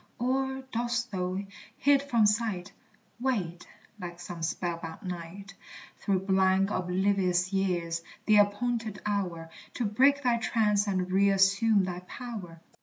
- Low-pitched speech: No, high, 195 Hz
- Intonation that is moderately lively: Yes, average, 4.0 semitones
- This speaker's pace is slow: Yes, slow, 125 wpm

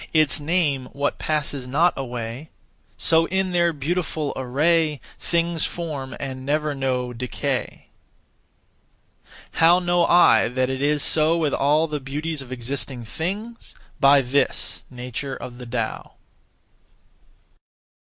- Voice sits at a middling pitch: Yes, medium, 145 Hz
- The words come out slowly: Yes, slow, 120 wpm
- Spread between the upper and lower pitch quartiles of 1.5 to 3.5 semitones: No, average, 3.9 semitones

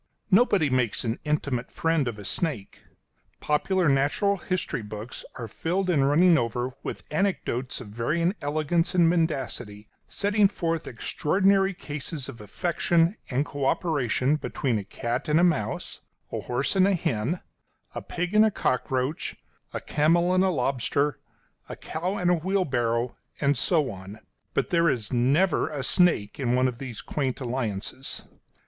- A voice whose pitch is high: No, medium, 145 Hz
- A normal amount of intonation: No, wide, 6.0 semitones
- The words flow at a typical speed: Yes, average, 155 wpm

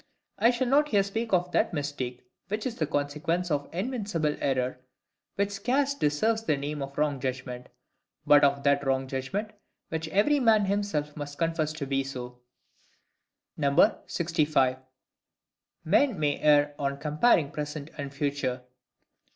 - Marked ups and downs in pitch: Yes, wide, 6.1 semitones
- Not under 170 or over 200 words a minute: No, average, 145 wpm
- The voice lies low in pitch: No, medium, 150 Hz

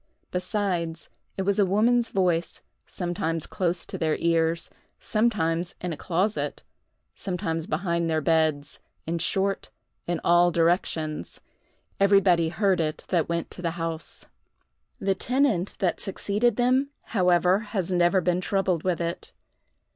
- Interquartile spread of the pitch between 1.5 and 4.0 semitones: Yes, average, 2.9 semitones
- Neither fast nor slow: No, slow, 130 wpm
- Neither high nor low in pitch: Yes, medium, 175 Hz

